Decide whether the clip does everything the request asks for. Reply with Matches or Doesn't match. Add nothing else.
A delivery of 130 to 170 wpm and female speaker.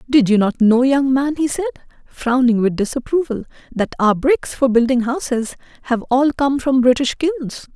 Doesn't match